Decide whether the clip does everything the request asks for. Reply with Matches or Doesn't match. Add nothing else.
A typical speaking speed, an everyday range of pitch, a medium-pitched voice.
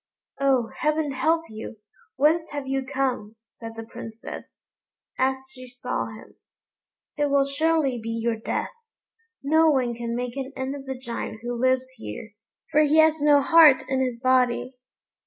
Doesn't match